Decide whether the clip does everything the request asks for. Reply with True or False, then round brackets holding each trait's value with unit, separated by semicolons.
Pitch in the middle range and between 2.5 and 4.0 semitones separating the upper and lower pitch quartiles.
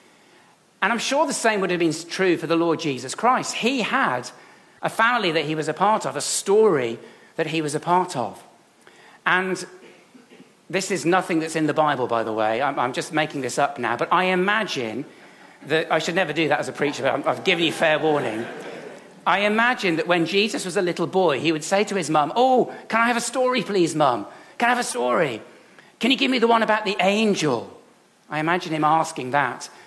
False (175 Hz; 5.6 semitones)